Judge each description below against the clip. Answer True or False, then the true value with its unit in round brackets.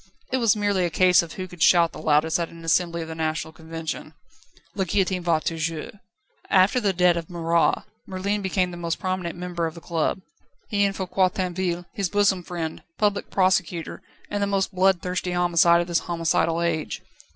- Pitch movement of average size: False (2.2 semitones)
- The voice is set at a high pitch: False (175 Hz)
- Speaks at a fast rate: False (185 wpm)